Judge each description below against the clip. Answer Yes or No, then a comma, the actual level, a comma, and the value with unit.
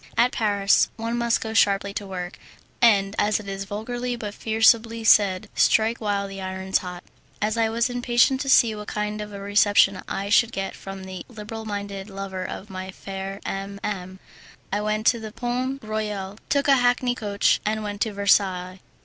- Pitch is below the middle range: No, high, 210 Hz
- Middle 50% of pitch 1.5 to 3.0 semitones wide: Yes, narrow, 2.4 semitones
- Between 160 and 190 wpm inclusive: Yes, average, 185 wpm